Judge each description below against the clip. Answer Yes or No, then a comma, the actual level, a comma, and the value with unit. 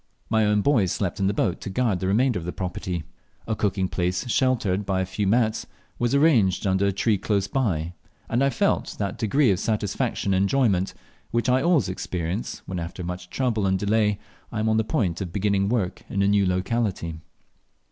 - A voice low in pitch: Yes, low, 100 Hz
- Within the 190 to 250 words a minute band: Yes, average, 200 wpm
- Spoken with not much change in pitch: No, average, 3.5 semitones